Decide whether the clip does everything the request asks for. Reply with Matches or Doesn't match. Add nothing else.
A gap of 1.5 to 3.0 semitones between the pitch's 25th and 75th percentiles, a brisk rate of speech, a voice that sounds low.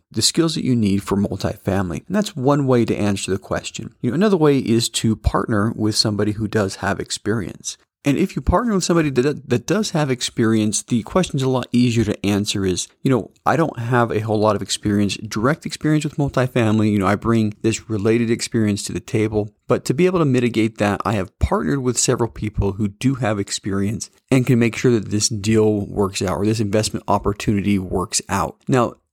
Doesn't match